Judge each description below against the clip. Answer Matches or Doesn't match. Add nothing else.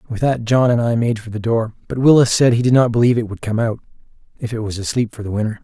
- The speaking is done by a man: Matches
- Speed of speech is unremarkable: Doesn't match